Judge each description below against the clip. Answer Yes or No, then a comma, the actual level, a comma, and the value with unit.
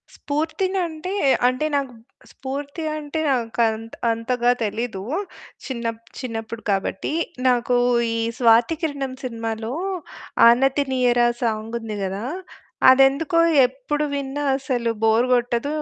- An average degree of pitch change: Yes, average, 3.6 semitones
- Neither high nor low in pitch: No, very high, 250 Hz